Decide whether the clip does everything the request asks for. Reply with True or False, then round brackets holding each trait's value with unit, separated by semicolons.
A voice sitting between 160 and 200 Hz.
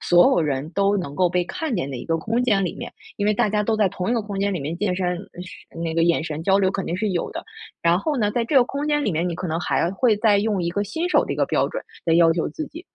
True (195 Hz)